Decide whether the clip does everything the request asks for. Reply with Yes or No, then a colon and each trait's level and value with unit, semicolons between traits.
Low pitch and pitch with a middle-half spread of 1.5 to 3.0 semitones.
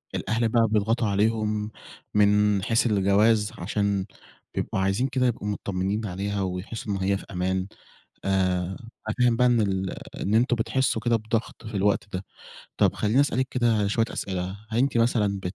Yes: low, 105 Hz; average, 2.7 semitones